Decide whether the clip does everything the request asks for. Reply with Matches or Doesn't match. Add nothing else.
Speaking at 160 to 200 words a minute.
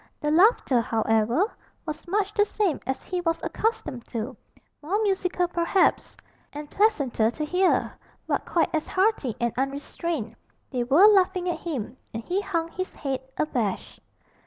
Doesn't match